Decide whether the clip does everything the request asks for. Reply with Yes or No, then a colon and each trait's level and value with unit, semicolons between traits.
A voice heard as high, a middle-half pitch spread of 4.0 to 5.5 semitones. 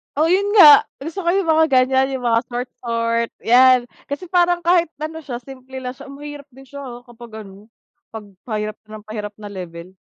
Yes: very high, 255 Hz; average, 4.5 semitones